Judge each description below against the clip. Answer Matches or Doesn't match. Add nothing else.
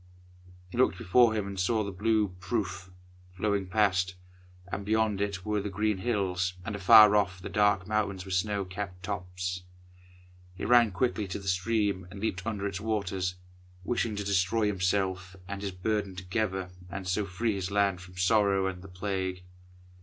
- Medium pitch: Doesn't match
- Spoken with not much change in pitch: Matches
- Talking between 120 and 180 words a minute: Matches